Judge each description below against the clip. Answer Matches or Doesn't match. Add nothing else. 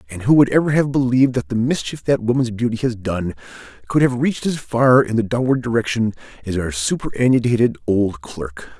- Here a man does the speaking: Matches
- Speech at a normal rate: Matches